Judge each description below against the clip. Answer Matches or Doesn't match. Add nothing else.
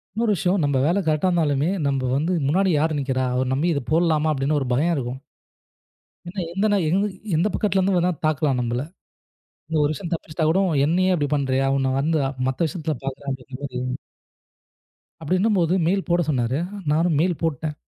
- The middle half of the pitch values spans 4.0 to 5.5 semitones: Matches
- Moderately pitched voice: Matches